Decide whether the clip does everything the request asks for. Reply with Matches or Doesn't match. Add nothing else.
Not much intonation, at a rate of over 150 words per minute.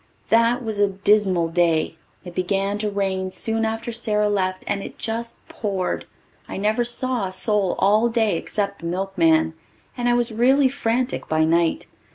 Doesn't match